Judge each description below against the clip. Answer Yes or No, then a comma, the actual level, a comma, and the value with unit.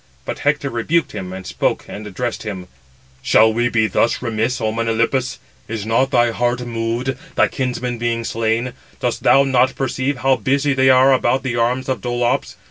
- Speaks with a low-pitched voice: Yes, low, 120 Hz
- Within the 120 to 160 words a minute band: No, average, 180 wpm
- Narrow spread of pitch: Yes, narrow, 2.3 semitones